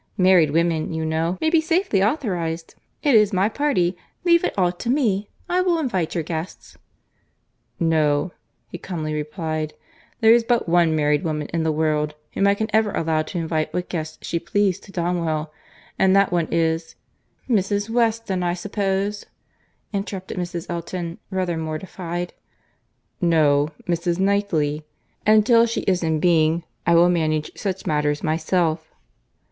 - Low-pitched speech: No, medium, 175 Hz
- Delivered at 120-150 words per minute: Yes, average, 145 wpm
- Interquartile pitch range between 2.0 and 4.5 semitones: Yes, average, 4.0 semitones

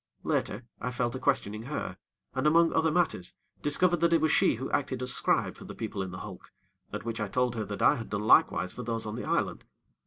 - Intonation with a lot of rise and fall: Yes, wide, 5.7 semitones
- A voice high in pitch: No, low, 125 Hz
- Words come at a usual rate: No, fast, 240 wpm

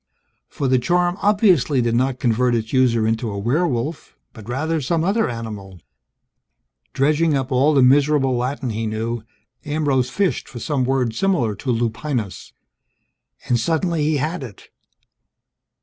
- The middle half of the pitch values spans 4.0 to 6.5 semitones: Yes, average, 4.7 semitones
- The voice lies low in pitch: Yes, low, 130 Hz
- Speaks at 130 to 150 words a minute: Yes, average, 145 wpm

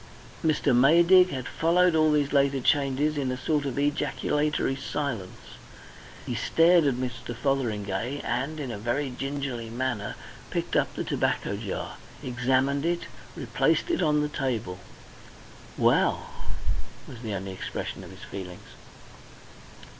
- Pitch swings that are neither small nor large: Yes, average, 3.8 semitones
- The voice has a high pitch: No, low, 135 Hz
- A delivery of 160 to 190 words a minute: No, slow, 135 wpm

